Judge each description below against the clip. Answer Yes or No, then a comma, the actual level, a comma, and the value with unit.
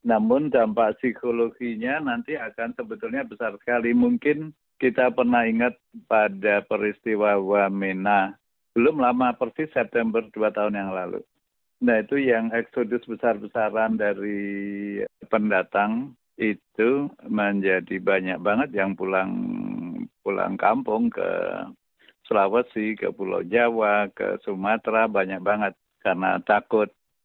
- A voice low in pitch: Yes, low, 115 Hz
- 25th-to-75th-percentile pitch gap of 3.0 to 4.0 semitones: Yes, average, 3.6 semitones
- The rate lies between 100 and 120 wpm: Yes, average, 110 wpm